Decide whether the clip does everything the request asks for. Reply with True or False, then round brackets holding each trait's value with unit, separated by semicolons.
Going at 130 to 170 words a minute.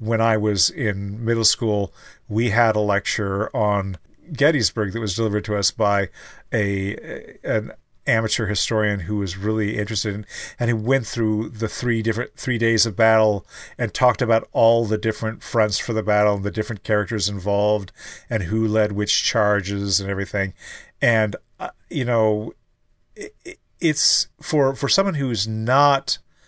True (160 wpm)